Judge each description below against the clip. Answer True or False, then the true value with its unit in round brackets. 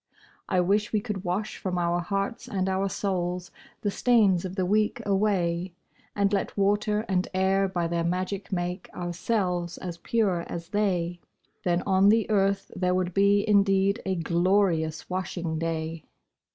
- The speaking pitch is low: False (190 Hz)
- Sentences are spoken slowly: False (155 wpm)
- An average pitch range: False (2.3 semitones)